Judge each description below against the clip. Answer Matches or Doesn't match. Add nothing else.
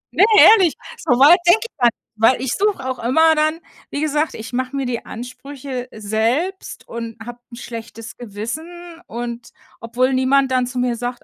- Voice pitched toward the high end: Matches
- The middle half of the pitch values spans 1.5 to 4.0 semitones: Doesn't match